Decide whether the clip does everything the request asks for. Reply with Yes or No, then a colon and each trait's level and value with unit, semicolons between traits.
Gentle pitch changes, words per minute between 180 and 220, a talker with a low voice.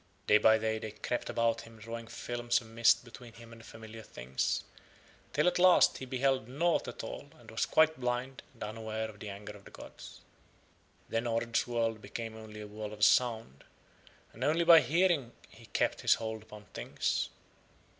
Yes: narrow, 2.2 semitones; average, 185 wpm; low, 115 Hz